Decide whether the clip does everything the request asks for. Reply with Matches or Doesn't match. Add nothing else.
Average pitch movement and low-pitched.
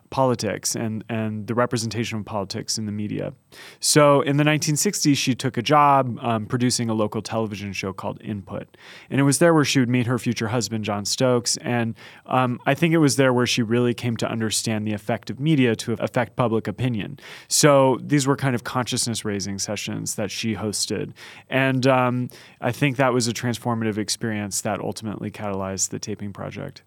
Matches